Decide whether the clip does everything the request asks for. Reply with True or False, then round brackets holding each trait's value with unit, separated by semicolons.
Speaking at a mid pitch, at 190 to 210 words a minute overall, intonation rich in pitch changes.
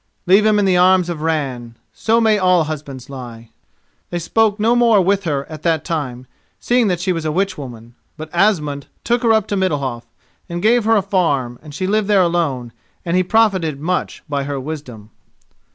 True (170 Hz; 195 wpm; 6.0 semitones)